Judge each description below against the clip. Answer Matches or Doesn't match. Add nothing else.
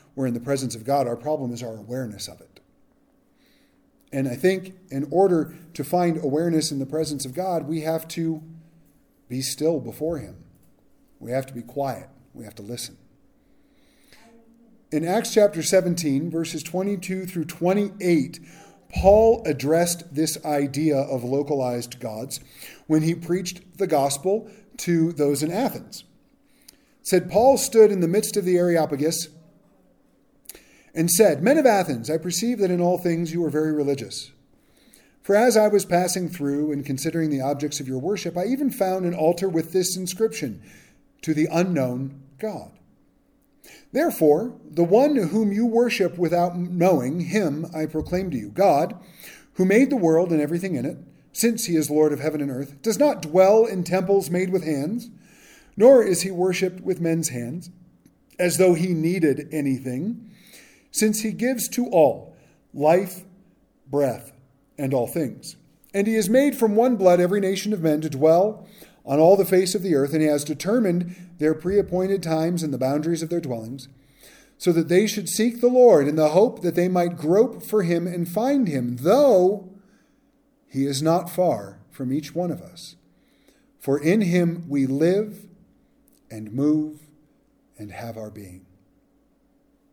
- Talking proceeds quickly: Doesn't match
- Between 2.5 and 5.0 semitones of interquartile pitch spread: Doesn't match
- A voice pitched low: Doesn't match